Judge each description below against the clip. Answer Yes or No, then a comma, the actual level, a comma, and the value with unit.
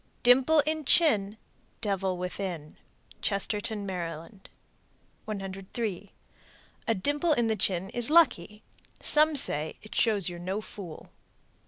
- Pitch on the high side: Yes, high, 205 Hz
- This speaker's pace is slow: Yes, slow, 115 wpm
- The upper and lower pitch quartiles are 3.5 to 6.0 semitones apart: Yes, average, 4.5 semitones